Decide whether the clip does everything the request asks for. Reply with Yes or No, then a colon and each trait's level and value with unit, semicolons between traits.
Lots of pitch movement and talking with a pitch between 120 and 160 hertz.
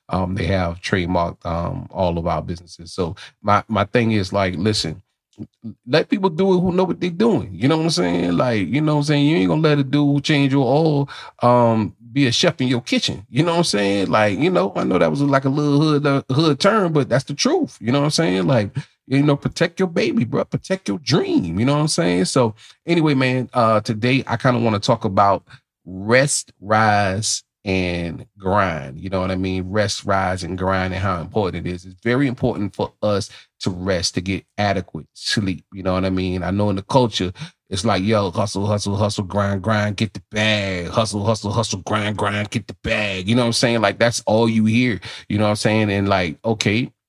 No: wide, 5.7 semitones; low, 110 Hz